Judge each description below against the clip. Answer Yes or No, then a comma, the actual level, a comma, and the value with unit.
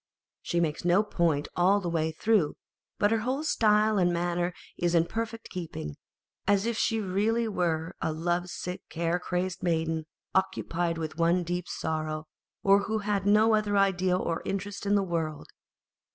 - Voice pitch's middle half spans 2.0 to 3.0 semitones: No, average, 3.5 semitones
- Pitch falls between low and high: Yes, medium, 180 Hz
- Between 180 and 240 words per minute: No, average, 165 wpm